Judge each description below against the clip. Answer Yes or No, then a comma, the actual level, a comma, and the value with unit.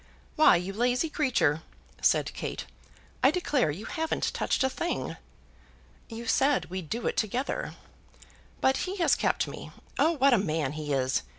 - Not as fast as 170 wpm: Yes, average, 160 wpm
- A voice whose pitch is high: Yes, high, 240 Hz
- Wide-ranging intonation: Yes, wide, 8.9 semitones